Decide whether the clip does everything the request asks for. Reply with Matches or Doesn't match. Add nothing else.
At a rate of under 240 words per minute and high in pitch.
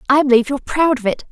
Doesn't match